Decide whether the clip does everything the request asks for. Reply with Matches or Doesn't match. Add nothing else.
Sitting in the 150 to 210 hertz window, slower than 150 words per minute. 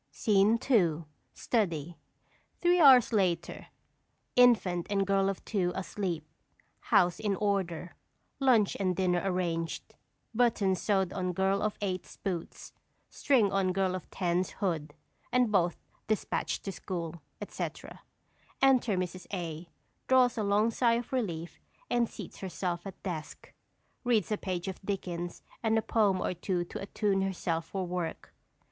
Matches